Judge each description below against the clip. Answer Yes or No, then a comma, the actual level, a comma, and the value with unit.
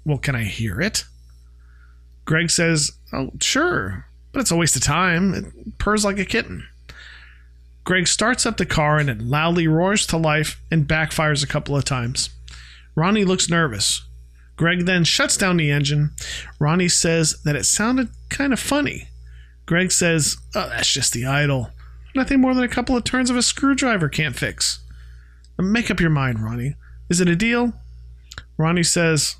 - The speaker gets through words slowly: No, average, 170 wpm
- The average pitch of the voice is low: No, medium, 150 Hz